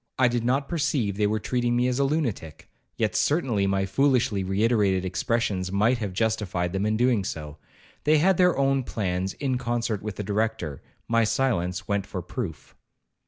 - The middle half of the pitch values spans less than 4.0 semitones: No, average, 4.7 semitones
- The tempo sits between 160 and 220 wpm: Yes, average, 165 wpm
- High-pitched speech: No, low, 110 Hz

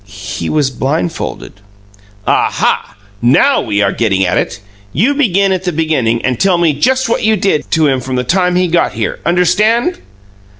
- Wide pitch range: Yes, wide, 8.3 semitones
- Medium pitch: Yes, medium, 160 Hz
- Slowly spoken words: No, average, 175 wpm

